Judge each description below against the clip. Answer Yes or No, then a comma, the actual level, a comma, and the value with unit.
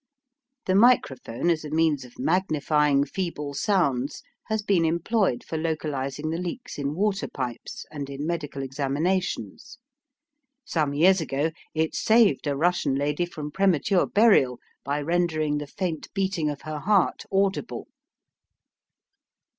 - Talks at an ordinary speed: No, slow, 130 wpm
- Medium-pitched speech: Yes, medium, 155 Hz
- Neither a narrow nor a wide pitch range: Yes, average, 4.6 semitones